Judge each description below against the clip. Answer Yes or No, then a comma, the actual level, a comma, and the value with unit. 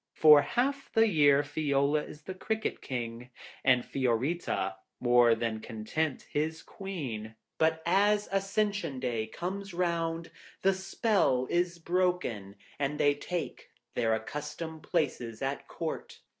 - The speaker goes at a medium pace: No, slow, 130 wpm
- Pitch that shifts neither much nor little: No, wide, 6.3 semitones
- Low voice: No, medium, 150 Hz